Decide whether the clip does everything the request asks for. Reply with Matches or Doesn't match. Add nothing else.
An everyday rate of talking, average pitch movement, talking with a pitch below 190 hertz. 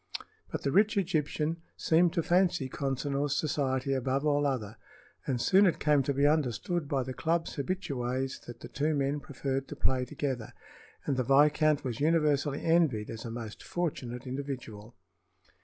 Matches